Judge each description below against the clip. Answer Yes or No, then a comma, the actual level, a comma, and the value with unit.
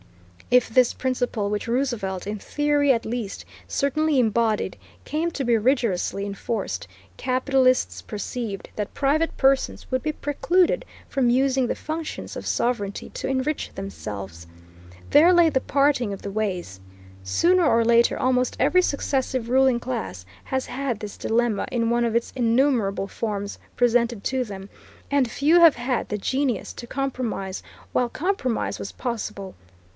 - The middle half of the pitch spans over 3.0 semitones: Yes, average, 4.5 semitones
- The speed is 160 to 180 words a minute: No, average, 145 wpm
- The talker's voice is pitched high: Yes, high, 245 Hz